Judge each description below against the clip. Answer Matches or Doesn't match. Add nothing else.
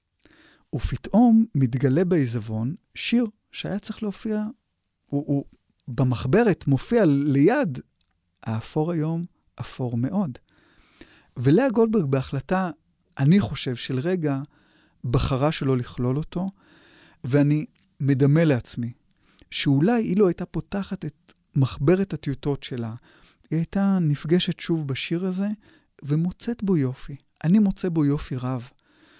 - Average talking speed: Matches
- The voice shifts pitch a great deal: Matches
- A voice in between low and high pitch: Matches